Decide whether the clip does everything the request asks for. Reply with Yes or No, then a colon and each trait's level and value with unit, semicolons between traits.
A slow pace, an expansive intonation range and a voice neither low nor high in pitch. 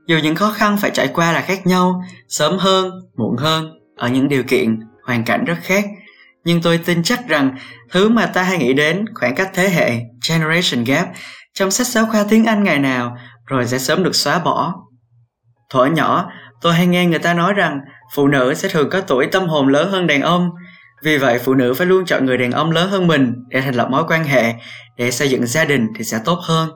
No: average, 230 wpm; wide, 6.4 semitones; medium, 160 Hz